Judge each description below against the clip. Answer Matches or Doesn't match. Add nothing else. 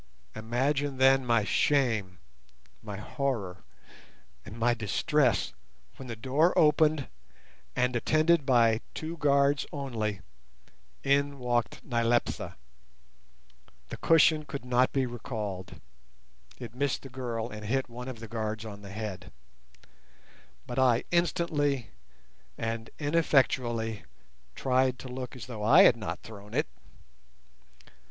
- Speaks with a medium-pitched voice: Doesn't match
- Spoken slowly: Matches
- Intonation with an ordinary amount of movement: Matches